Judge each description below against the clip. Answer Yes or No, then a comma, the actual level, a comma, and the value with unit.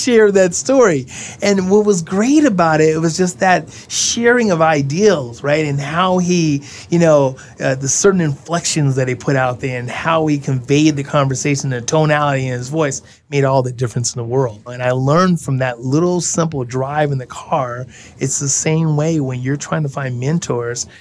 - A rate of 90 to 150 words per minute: No, average, 200 wpm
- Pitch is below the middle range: No, medium, 145 Hz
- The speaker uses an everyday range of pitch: Yes, average, 4.3 semitones